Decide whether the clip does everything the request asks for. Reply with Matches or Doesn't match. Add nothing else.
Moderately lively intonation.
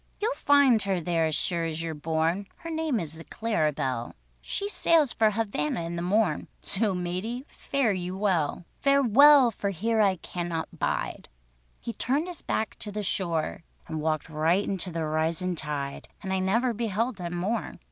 Doesn't match